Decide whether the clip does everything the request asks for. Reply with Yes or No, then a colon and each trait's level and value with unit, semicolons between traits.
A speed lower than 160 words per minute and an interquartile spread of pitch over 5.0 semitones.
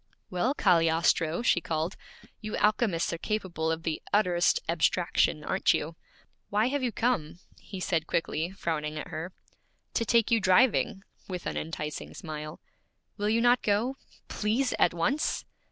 Yes: average, 150 wpm; wide, 5.6 semitones